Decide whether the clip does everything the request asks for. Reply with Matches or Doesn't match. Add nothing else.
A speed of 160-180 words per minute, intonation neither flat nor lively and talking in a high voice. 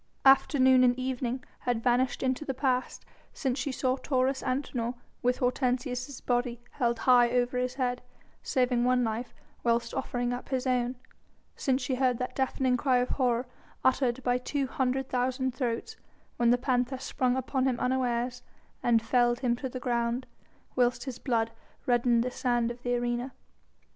Doesn't match